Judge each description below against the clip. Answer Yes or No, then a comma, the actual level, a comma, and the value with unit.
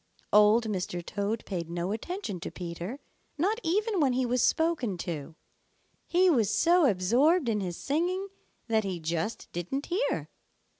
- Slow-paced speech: No, average, 150 wpm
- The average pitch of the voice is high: Yes, high, 225 Hz